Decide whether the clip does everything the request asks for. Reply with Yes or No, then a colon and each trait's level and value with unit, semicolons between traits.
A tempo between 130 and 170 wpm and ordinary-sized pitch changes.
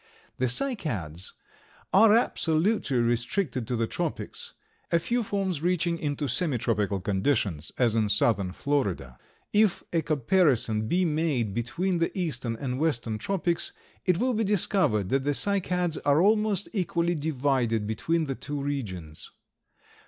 No: slow, 135 wpm; wide, 7.7 semitones